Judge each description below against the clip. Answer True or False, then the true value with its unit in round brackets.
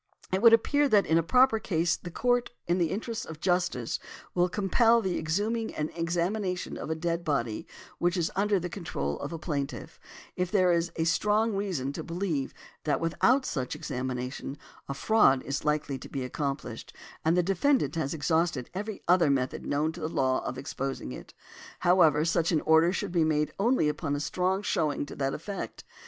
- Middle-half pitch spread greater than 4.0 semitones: True (4.8 semitones)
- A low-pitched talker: False (170 Hz)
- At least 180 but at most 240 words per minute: True (190 wpm)